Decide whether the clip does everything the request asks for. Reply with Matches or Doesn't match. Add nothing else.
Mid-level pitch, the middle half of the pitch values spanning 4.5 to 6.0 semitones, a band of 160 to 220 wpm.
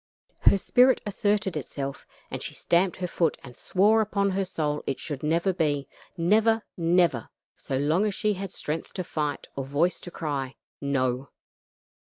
Matches